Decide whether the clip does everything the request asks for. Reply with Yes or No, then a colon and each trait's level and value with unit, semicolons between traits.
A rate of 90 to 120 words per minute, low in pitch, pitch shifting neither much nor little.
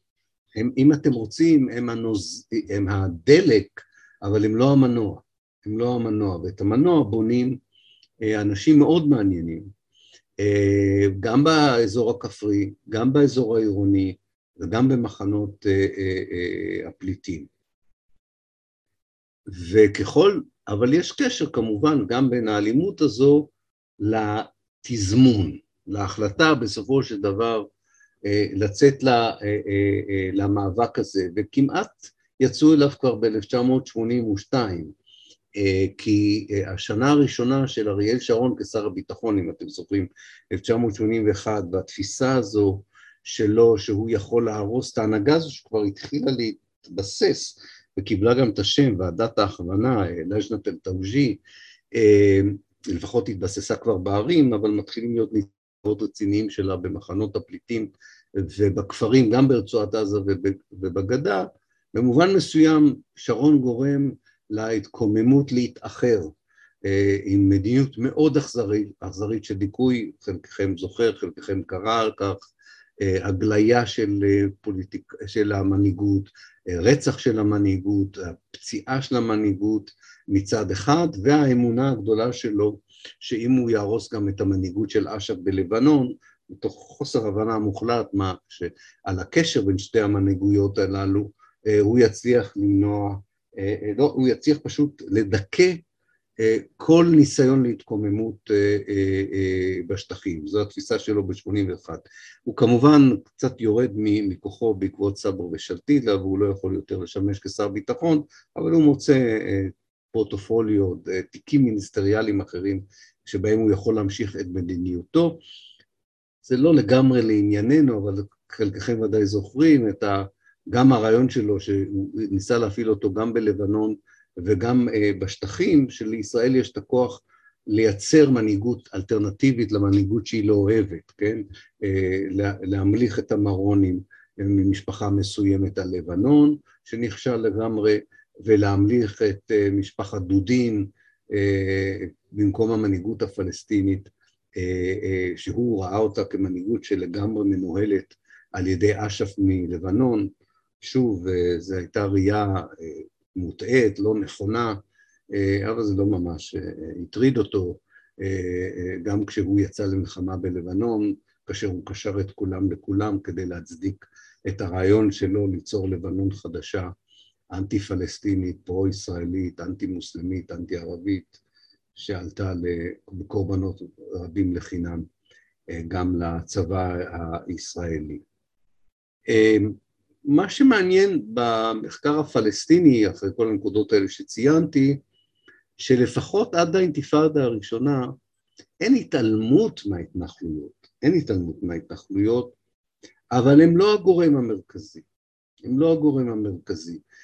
Yes: slow, 100 wpm; low, 105 Hz; average, 3.9 semitones